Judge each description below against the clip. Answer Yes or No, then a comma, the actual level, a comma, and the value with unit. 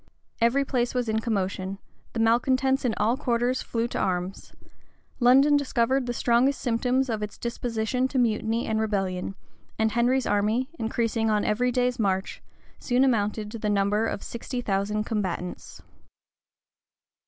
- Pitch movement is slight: No, average, 3.0 semitones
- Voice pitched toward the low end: No, high, 230 Hz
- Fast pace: No, average, 145 wpm